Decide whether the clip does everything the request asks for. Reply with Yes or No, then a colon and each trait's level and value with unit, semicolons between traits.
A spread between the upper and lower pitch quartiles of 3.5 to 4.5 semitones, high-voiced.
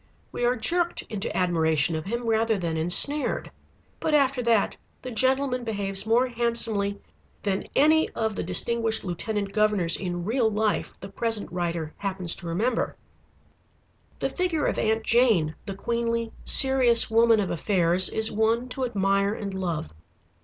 Yes: average, 3.9 semitones; high, 220 Hz